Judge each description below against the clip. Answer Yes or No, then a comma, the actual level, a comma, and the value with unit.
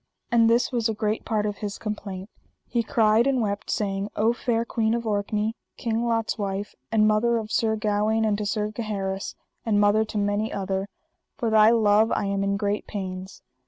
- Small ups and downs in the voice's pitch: Yes, narrow, 1.8 semitones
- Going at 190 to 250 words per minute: Yes, average, 195 wpm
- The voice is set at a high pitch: Yes, high, 215 Hz